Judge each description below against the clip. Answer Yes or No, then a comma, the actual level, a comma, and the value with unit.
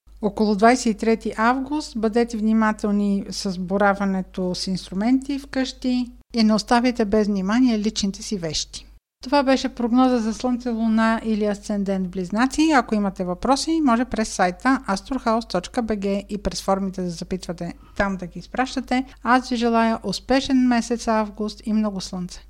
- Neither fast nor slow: Yes, average, 145 wpm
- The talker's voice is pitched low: No, high, 220 Hz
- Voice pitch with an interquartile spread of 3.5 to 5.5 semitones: Yes, average, 3.9 semitones